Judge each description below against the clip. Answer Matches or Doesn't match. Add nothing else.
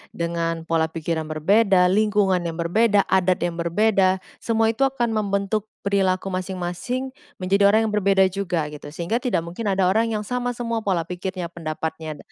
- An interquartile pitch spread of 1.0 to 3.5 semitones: Doesn't match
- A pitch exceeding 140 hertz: Matches